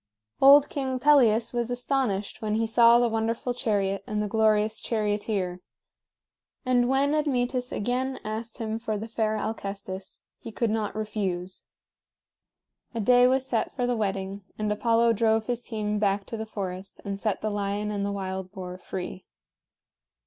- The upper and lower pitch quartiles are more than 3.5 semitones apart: No, average, 3.1 semitones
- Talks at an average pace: Yes, average, 160 wpm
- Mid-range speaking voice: No, high, 220 Hz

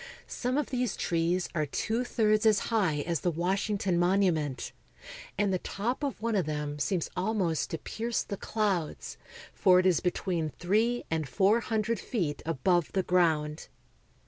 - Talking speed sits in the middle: Yes, average, 150 wpm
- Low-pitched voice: No, medium, 185 Hz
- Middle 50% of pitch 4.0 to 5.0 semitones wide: Yes, average, 4.7 semitones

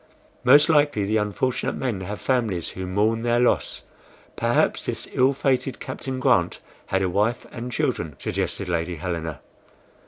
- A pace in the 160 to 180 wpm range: No, average, 150 wpm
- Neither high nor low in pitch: No, low, 110 Hz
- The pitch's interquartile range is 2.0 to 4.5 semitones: No, wide, 5.4 semitones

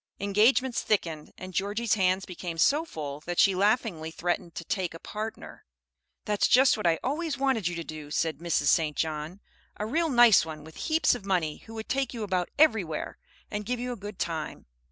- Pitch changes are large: Yes, wide, 5.8 semitones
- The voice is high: Yes, high, 195 Hz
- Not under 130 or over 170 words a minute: No, average, 195 wpm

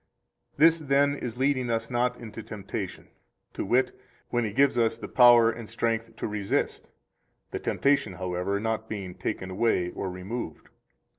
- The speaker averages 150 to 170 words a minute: Yes, average, 155 wpm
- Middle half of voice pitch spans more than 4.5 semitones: No, average, 3.7 semitones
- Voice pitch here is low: Yes, low, 115 Hz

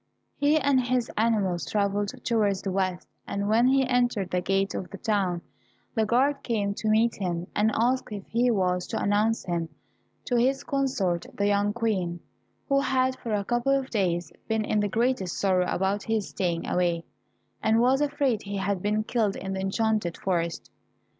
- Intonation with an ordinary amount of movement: Yes, average, 4.0 semitones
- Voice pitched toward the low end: No, high, 210 Hz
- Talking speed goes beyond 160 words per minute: Yes, average, 180 wpm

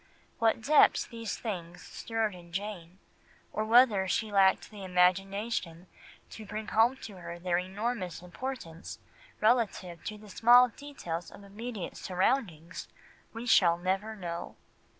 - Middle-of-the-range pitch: No, high, 200 Hz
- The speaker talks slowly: Yes, slow, 130 wpm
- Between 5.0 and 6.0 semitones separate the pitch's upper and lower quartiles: No, average, 4.0 semitones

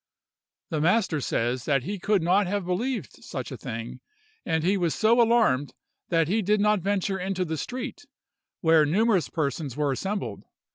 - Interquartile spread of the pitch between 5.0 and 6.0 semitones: Yes, average, 5.3 semitones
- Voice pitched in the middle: Yes, medium, 180 Hz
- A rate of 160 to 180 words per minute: Yes, average, 170 wpm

